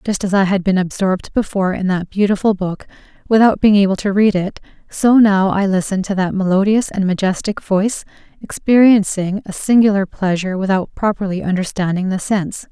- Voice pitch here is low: No, high, 195 Hz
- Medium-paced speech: Yes, average, 170 wpm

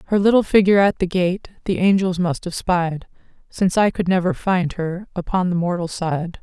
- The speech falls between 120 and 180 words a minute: No, average, 195 wpm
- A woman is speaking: Yes, female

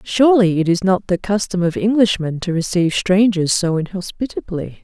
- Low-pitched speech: No, high, 190 Hz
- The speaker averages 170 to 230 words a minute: No, average, 160 wpm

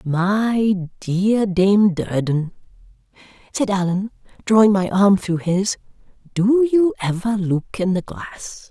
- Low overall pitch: No, high, 200 Hz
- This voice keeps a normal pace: No, slow, 125 wpm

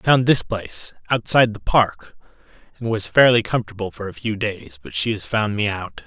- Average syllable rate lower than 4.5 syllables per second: No, 5.4 syllables/s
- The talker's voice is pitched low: Yes, low, 105 Hz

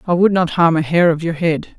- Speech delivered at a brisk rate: Yes, fast, 300 wpm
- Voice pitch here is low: No, medium, 170 Hz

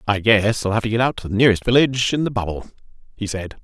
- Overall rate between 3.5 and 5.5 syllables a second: No, 7.0 syllables/s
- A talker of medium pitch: No, low, 110 Hz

